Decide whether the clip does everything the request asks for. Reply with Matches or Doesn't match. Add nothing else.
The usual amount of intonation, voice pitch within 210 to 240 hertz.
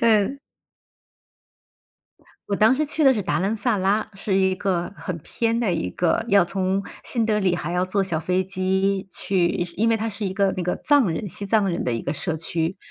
Doesn't match